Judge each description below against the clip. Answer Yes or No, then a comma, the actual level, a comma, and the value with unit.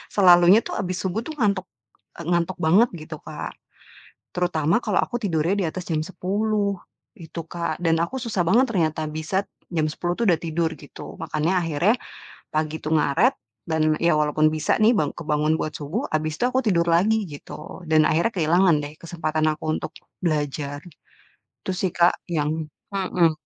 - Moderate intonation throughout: Yes, average, 3.2 semitones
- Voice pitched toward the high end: No, medium, 170 Hz